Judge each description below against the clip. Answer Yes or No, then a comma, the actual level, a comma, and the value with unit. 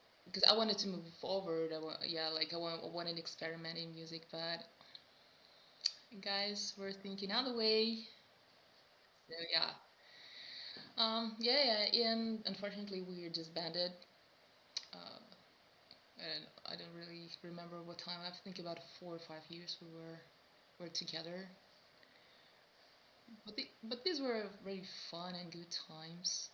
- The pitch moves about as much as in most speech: Yes, average, 3.6 semitones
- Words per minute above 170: No, average, 145 wpm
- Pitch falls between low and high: Yes, medium, 175 Hz